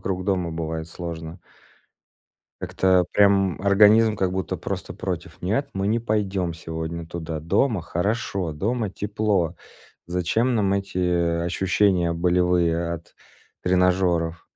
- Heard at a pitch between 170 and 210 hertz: No, very low, 90 Hz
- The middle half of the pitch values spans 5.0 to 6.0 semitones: No, average, 2.9 semitones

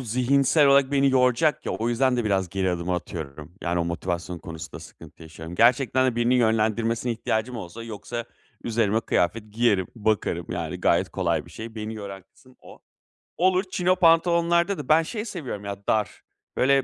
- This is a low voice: Yes, low, 115 Hz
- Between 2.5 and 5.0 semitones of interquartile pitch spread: No, wide, 5.5 semitones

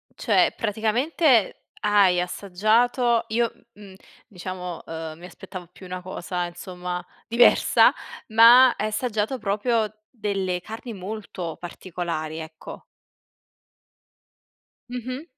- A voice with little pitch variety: No, average, 4.3 semitones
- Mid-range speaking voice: No, high, 205 Hz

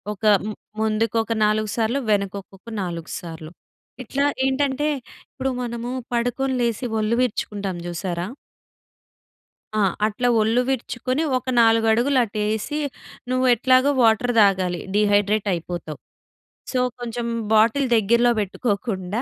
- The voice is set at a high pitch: Yes, high, 220 Hz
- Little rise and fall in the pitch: No, average, 3.6 semitones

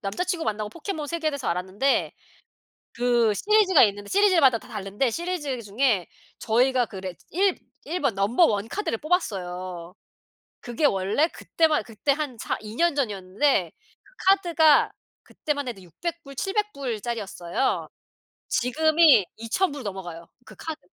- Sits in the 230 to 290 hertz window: Yes, very high, 250 Hz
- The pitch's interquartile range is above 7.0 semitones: Yes, wide, 7.8 semitones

